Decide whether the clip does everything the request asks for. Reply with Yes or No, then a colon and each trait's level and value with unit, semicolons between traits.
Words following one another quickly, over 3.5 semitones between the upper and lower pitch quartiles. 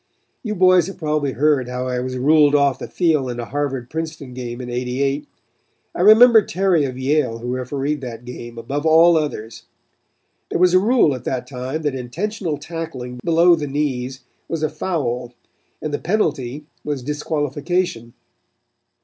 No: average, 165 wpm; average, 4.3 semitones